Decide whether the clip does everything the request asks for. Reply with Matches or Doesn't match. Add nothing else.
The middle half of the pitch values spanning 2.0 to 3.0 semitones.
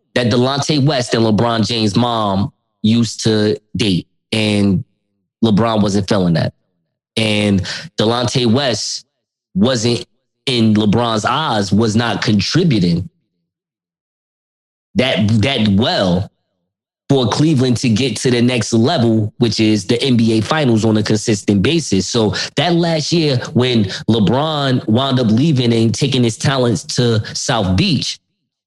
Doesn't match